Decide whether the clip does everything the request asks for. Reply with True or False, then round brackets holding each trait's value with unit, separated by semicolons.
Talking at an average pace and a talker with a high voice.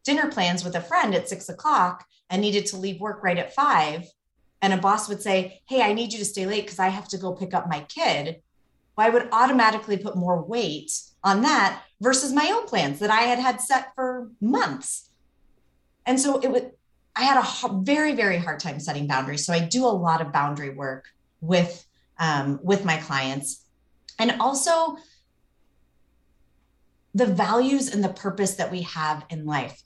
True (190 wpm; 195 Hz)